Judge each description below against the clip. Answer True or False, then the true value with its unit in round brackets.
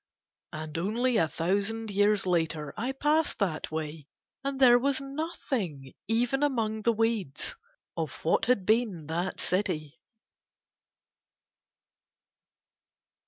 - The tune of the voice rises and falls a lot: True (7.1 semitones)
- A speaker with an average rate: False (110 wpm)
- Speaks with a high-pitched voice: True (210 Hz)